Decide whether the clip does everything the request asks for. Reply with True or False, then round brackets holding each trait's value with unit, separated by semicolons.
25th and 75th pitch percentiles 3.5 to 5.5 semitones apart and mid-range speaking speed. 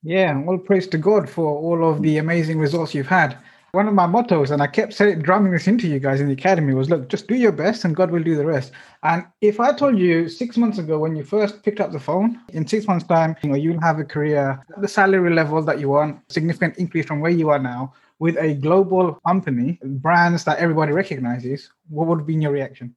False (4.0 semitones; 245 wpm)